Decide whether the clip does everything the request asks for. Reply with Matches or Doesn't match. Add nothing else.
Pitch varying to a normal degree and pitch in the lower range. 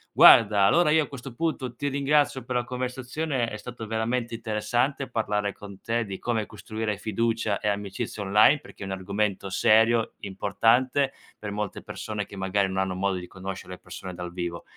Matches